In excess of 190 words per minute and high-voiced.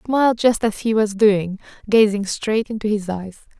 Yes: average, 200 wpm; high, 210 Hz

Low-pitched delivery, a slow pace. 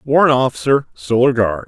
Yes: low, 125 Hz; slow, 110 wpm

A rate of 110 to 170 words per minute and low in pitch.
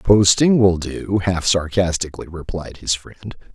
Yes: slow, 135 wpm; very low, 95 Hz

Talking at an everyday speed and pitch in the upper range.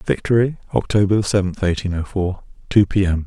No: average, 165 wpm; very low, 95 Hz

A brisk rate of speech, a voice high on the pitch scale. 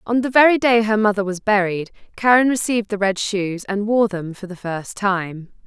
Yes: fast, 210 wpm; high, 205 Hz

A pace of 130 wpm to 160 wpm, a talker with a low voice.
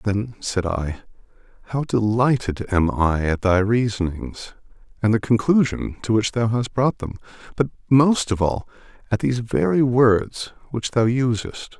Yes: average, 155 wpm; low, 110 Hz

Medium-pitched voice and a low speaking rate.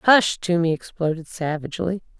Yes: medium, 175 Hz; slow, 110 wpm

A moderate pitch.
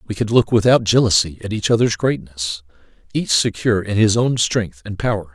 No: low, 105 Hz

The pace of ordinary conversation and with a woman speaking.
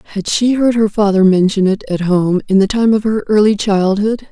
No: fast, 225 wpm; female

